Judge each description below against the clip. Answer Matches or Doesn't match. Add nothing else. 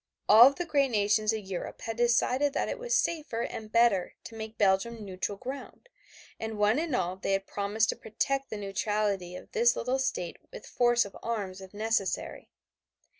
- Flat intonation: Doesn't match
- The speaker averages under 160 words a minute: Doesn't match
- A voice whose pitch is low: Doesn't match